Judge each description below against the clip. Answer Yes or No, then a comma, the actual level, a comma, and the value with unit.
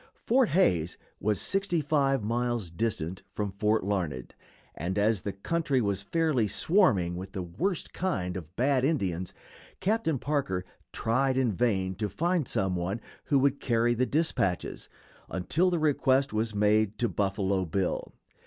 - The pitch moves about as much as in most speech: No, wide, 6.9 semitones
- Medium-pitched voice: No, low, 110 Hz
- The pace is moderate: Yes, average, 150 wpm